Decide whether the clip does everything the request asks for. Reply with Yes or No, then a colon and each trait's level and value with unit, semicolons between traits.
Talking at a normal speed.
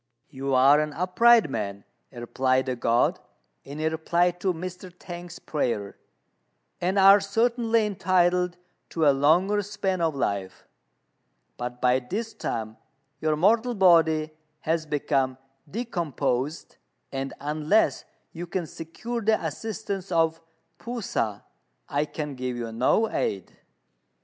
No: slow, 125 wpm